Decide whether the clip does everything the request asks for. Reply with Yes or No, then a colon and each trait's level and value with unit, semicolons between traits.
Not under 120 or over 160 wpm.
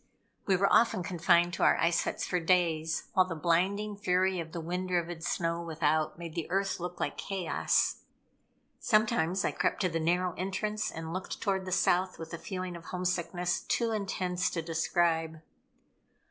No: average, 175 wpm